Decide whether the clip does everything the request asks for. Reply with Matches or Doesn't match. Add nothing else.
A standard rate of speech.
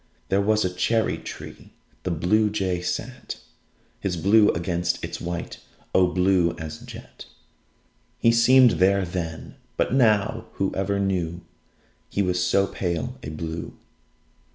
Doesn't match